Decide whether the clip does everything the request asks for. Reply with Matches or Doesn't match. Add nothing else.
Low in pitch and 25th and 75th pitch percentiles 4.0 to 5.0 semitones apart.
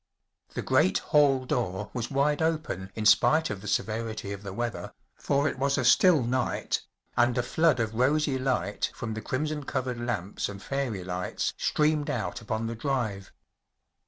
Matches